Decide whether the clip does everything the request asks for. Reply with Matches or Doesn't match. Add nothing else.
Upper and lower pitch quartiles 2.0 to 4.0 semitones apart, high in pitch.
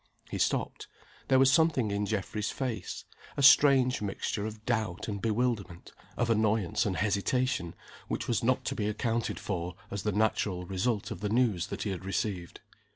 Doesn't match